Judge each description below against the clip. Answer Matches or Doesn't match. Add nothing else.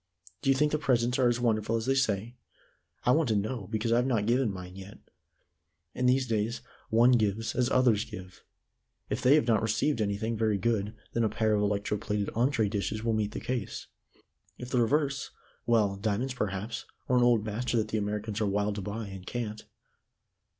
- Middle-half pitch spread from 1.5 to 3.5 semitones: Matches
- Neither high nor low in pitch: Doesn't match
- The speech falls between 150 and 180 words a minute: Doesn't match